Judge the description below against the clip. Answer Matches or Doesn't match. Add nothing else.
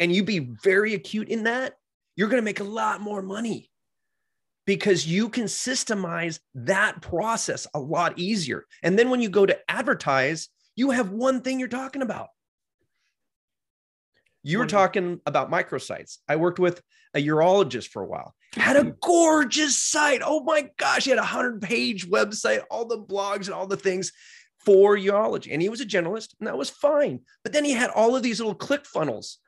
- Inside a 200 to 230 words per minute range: Doesn't match